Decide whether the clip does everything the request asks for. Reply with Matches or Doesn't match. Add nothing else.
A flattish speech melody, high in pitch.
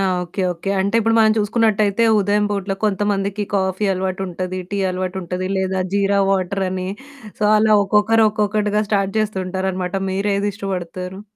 Matches